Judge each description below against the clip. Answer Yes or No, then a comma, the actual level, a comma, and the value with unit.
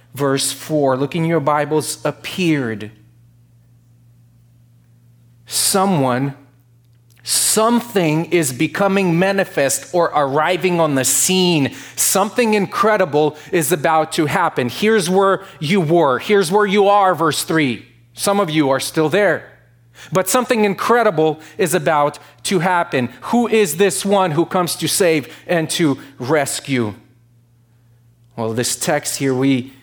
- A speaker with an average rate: No, slow, 125 wpm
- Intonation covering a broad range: Yes, wide, 6.9 semitones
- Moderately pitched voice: Yes, medium, 150 Hz